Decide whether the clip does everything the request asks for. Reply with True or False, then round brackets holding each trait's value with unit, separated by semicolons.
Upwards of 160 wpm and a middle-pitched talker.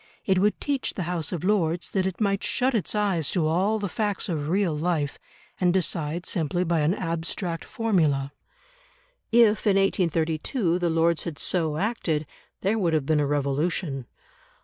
True (170 wpm; 175 Hz)